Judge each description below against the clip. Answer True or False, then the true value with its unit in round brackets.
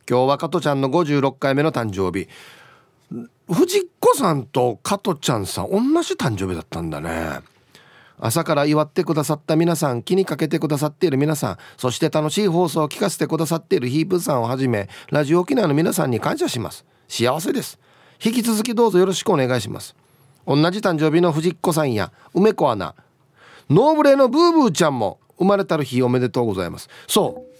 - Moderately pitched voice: True (155 Hz)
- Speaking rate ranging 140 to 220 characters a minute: False (390 characters per minute)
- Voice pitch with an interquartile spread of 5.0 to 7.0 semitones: True (6.3 semitones)